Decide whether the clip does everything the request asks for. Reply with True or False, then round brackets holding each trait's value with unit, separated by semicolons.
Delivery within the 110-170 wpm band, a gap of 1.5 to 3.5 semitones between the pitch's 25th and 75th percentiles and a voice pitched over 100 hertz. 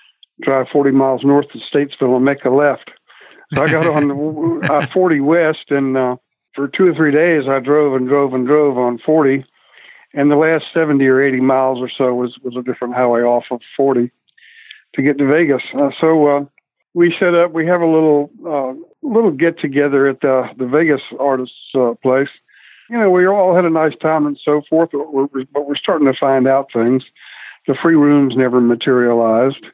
False (200 wpm; 3.1 semitones; 140 Hz)